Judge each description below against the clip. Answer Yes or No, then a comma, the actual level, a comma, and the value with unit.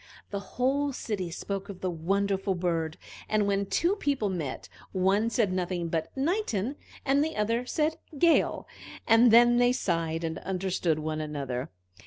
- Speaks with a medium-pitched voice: No, high, 200 Hz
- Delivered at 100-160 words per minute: Yes, average, 155 wpm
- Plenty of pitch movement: Yes, wide, 6.0 semitones